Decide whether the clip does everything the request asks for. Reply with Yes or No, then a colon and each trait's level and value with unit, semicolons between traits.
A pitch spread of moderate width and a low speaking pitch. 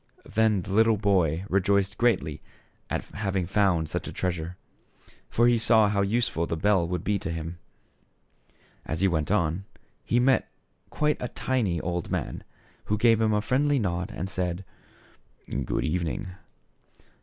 Yes: average, 4.2 semitones; low, 100 Hz